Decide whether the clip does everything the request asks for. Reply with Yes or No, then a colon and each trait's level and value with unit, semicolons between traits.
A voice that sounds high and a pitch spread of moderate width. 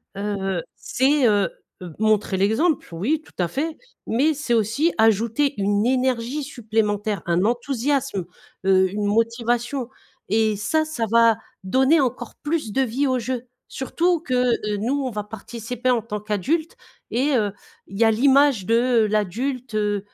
Yes: high, 230 Hz; average, 4.2 semitones